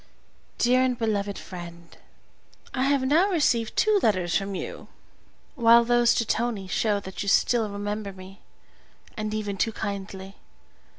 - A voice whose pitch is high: Yes, high, 215 Hz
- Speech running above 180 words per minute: No, average, 140 wpm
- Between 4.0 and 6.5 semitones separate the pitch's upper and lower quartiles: No, average, 3.5 semitones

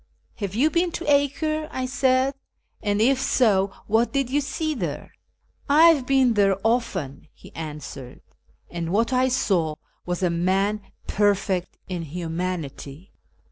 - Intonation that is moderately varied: No, wide, 6.8 semitones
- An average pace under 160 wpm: No, average, 170 wpm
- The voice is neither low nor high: No, high, 210 Hz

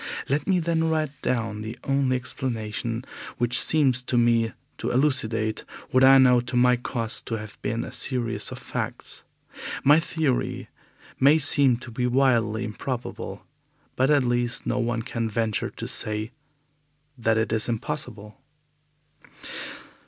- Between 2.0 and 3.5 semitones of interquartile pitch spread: Yes, average, 2.9 semitones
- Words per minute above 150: No, average, 145 wpm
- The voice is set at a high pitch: No, low, 120 Hz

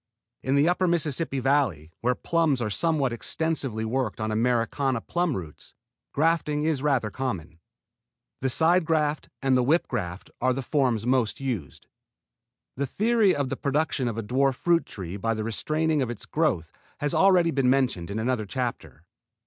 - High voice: No, low, 130 Hz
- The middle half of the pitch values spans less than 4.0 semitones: No, average, 5.3 semitones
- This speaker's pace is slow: No, average, 165 wpm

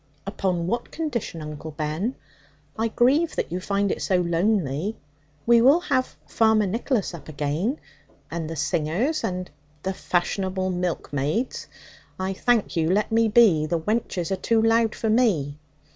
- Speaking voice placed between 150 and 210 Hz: Yes, high, 190 Hz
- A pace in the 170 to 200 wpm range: No, average, 155 wpm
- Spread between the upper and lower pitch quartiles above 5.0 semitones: Yes, wide, 5.5 semitones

